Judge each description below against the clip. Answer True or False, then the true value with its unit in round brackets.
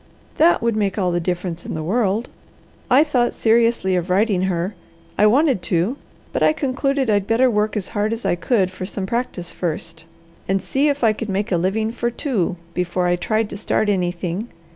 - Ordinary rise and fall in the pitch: True (4.6 semitones)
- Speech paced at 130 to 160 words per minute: False (200 wpm)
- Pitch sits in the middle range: False (205 Hz)